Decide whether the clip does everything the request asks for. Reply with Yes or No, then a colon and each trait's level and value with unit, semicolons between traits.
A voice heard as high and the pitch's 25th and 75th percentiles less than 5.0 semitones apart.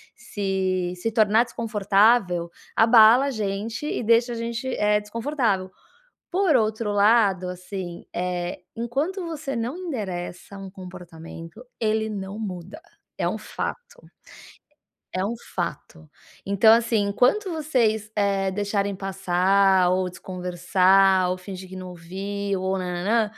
Yes: high, 200 Hz; average, 3.7 semitones